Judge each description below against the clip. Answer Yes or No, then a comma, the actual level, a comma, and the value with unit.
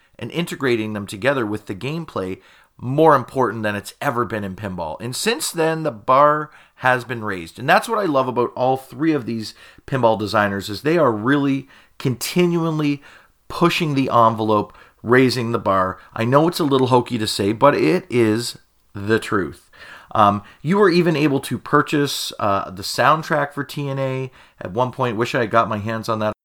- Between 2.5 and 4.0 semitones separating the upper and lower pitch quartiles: No, average, 4.8 semitones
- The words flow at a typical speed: Yes, average, 185 wpm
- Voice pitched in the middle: No, low, 125 Hz